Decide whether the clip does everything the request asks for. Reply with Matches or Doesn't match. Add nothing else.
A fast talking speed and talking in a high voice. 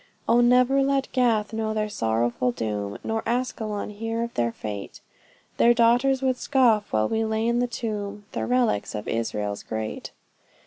Doesn't match